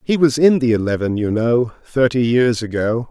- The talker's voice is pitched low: Yes, low, 120 Hz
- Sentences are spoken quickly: No, average, 195 wpm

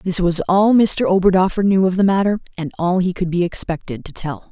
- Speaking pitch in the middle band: Yes, medium, 180 Hz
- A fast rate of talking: Yes, fast, 225 wpm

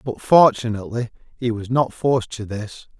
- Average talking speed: Yes, average, 160 wpm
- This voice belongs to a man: Yes, male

